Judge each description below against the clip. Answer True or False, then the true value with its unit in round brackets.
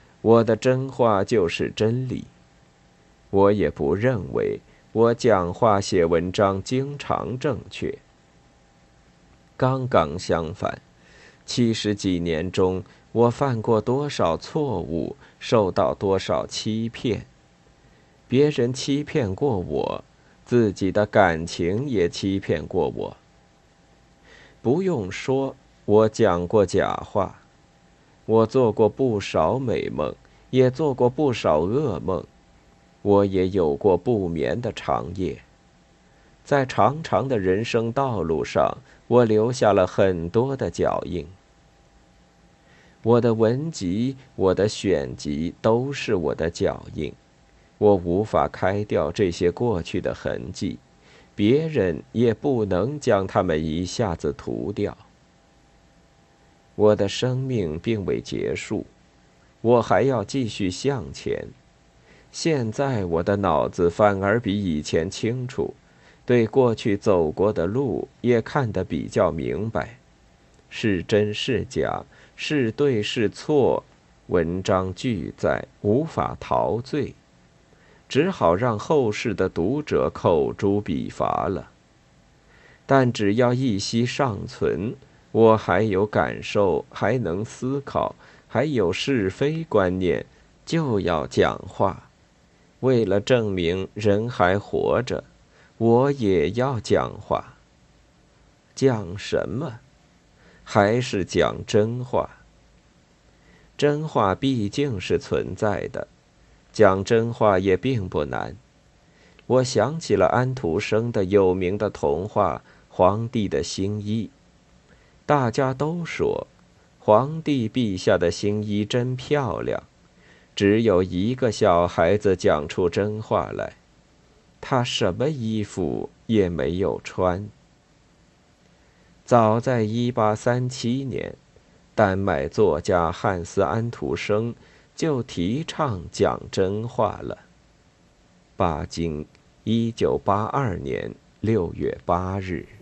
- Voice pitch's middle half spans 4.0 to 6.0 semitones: True (5.3 semitones)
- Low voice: True (105 Hz)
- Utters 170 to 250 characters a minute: False (155 characters per minute)